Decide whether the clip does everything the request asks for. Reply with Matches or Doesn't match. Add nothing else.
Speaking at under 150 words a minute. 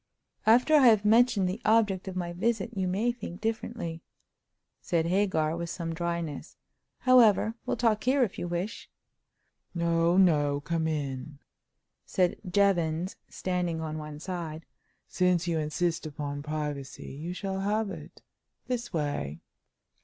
Matches